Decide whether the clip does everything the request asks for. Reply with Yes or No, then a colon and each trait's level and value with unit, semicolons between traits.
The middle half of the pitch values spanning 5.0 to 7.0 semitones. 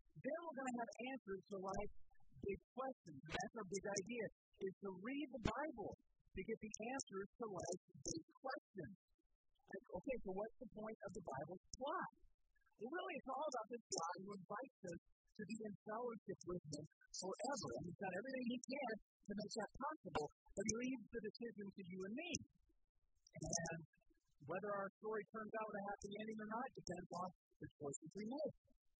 No: average, 4.6 semitones